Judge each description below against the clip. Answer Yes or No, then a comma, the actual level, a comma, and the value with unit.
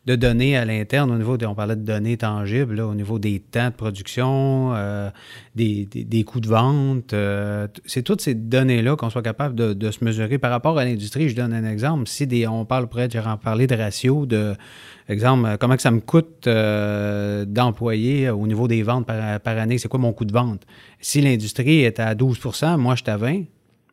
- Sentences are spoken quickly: Yes, fast, 220 wpm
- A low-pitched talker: Yes, low, 115 Hz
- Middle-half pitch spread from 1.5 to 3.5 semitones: Yes, average, 3.0 semitones